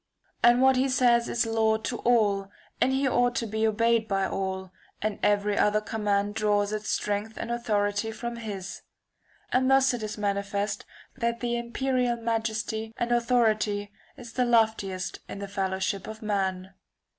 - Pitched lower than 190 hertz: No, high, 220 Hz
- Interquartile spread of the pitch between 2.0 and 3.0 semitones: Yes, average, 2.7 semitones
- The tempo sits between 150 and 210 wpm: Yes, average, 165 wpm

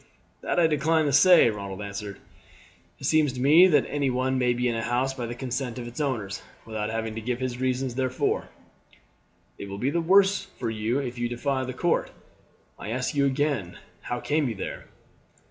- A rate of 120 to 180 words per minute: No, average, 200 wpm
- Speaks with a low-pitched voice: Yes, low, 125 Hz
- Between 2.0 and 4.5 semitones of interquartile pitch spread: Yes, average, 3.7 semitones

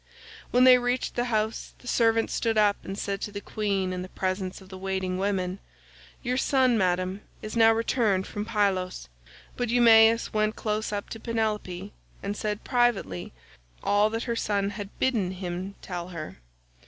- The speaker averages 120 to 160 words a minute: No, average, 170 wpm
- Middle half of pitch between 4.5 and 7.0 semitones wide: No, average, 3.2 semitones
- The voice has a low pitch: No, high, 210 Hz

